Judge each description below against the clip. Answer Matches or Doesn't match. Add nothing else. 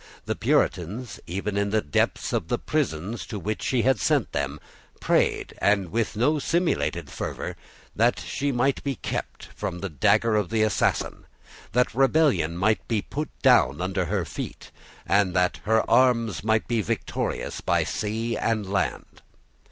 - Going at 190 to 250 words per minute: Doesn't match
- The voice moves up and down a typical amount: Matches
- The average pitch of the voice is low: Matches